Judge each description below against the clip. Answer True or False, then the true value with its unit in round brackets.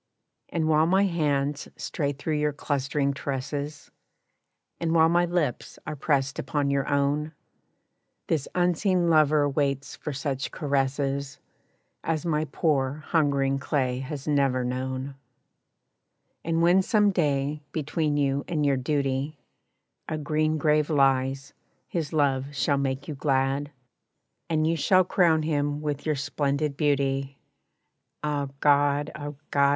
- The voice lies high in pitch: False (145 Hz)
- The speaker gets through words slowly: True (130 wpm)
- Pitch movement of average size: False (2.1 semitones)